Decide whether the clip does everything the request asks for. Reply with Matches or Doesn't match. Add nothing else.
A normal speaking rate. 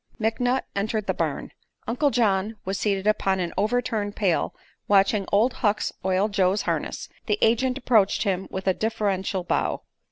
Matches